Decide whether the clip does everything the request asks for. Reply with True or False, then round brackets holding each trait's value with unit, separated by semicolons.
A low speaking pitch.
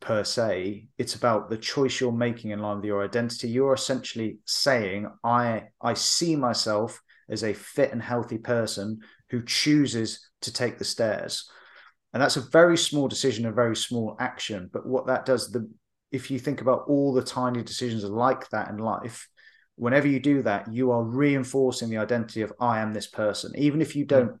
True (120 Hz)